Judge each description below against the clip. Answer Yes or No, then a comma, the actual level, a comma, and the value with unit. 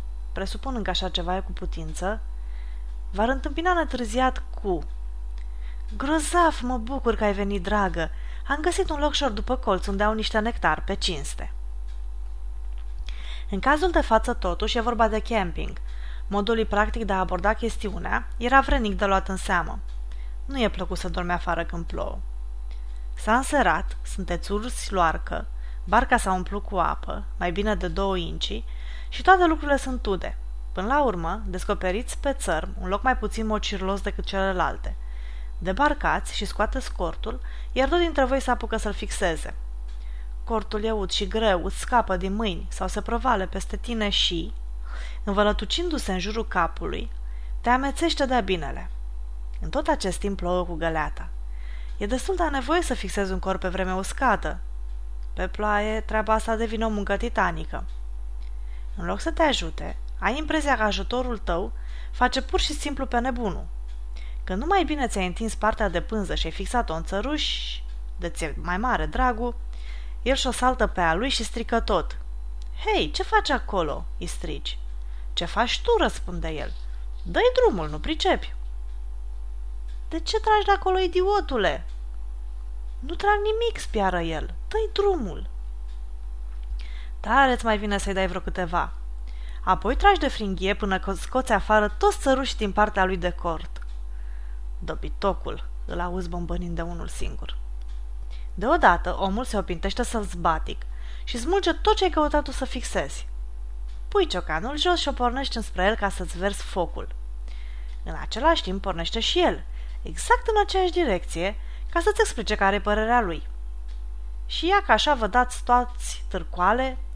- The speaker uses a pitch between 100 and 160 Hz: No, high, 195 Hz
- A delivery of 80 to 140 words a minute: No, average, 155 wpm